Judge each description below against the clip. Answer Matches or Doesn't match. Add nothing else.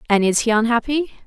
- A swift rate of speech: Doesn't match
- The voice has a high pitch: Matches